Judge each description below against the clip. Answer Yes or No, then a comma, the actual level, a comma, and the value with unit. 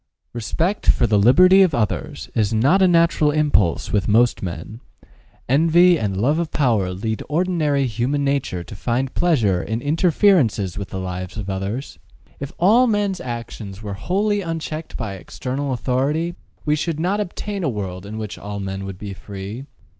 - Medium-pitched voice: No, low, 125 Hz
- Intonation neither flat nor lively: No, wide, 8.2 semitones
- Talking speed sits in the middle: Yes, average, 170 wpm